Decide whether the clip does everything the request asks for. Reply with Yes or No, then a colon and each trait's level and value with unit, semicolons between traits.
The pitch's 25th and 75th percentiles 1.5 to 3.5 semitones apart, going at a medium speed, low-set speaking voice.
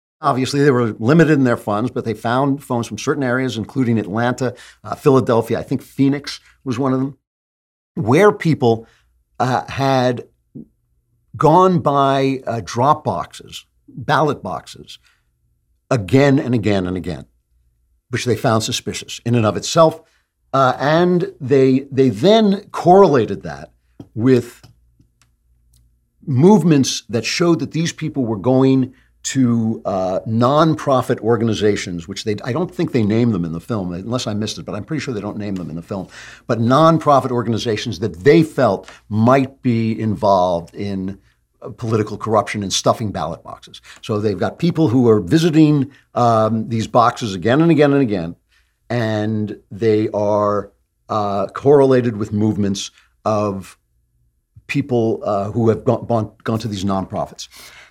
No: average, 4.7 semitones; average, 145 wpm; low, 115 Hz